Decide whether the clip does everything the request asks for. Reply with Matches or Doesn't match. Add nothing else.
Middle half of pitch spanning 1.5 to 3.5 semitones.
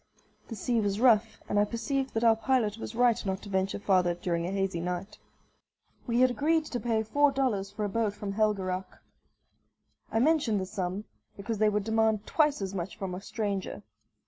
Matches